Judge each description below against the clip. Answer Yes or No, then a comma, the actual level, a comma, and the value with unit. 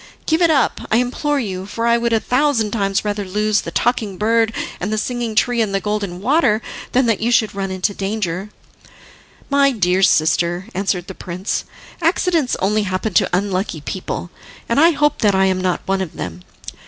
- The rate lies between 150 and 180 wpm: No, average, 190 wpm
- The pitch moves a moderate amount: Yes, average, 4.1 semitones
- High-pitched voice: Yes, high, 210 Hz